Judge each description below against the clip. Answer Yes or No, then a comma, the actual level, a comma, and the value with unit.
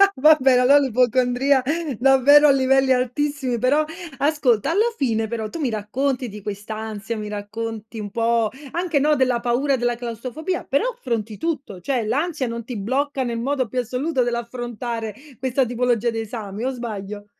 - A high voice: Yes, high, 245 Hz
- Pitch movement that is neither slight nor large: Yes, average, 3.4 semitones